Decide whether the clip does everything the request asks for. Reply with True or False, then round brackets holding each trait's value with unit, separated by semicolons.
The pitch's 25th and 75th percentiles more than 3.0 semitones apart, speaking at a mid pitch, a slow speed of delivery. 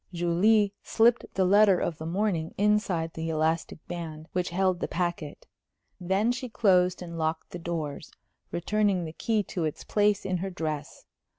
False (3.8 semitones; 180 Hz; 165 wpm)